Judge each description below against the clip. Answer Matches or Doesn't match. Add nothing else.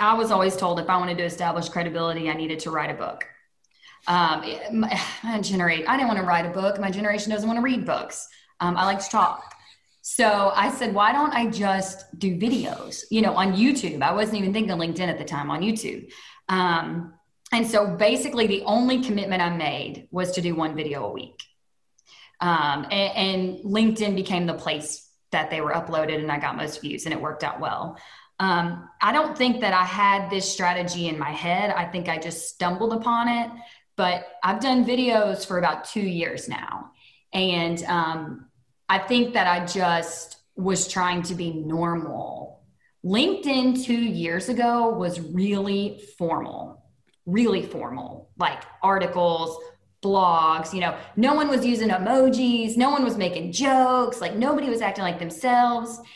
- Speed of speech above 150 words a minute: Matches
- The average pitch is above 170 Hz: Matches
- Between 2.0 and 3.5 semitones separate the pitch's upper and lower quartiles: Doesn't match